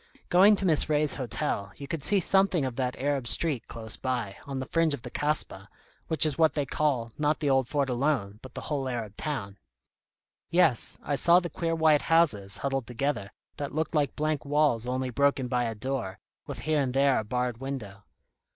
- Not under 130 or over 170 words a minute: No, average, 200 wpm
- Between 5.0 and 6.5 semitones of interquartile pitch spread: No, average, 4.1 semitones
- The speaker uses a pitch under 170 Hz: Yes, low, 135 Hz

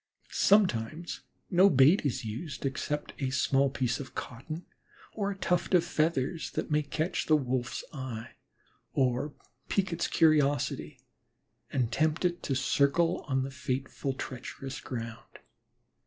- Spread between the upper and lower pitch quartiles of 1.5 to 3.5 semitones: No, average, 4.1 semitones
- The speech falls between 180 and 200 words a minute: No, slow, 135 wpm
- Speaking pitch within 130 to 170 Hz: Yes, medium, 140 Hz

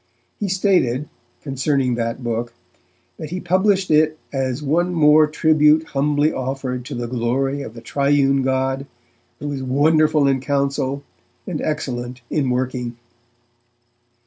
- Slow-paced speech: Yes, slow, 130 wpm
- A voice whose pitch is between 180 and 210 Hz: No, medium, 140 Hz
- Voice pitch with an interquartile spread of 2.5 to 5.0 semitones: Yes, average, 3.1 semitones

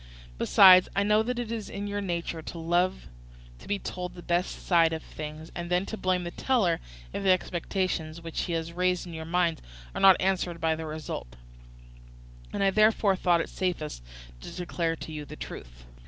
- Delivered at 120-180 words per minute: No, average, 195 wpm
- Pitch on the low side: No, medium, 175 Hz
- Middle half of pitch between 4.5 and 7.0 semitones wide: No, average, 2.8 semitones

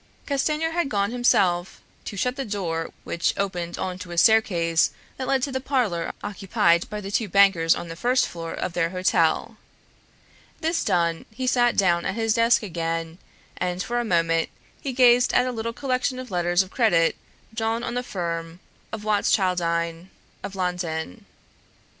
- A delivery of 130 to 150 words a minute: No, average, 170 wpm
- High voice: Yes, high, 195 Hz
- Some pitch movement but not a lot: No, wide, 5.9 semitones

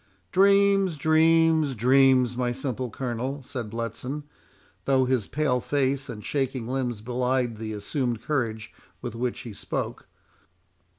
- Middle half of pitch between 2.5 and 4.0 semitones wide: Yes, average, 3.0 semitones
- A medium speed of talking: No, slow, 125 wpm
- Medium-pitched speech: No, low, 130 Hz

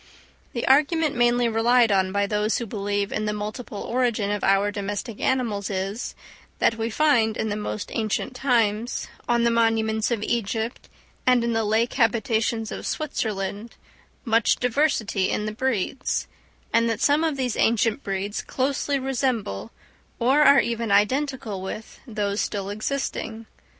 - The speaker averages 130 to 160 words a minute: Yes, average, 150 wpm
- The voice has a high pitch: Yes, high, 225 Hz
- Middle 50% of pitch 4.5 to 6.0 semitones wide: No, average, 3.1 semitones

